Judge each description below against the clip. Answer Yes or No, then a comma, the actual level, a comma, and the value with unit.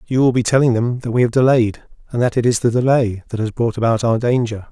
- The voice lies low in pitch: Yes, low, 120 Hz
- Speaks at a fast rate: Yes, fast, 265 wpm